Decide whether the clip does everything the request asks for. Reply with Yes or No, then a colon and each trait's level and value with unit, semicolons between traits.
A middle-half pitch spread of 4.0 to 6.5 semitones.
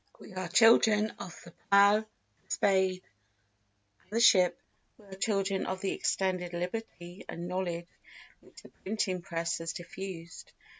No: narrow, 2.4 semitones